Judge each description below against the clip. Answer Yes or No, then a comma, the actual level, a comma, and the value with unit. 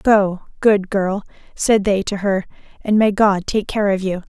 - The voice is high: Yes, high, 200 Hz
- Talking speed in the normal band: Yes, average, 195 wpm